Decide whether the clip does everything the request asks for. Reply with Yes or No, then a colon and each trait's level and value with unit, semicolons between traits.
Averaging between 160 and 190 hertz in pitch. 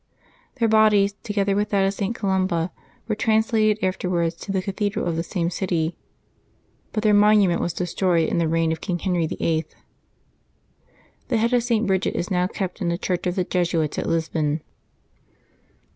Yes: medium, 185 Hz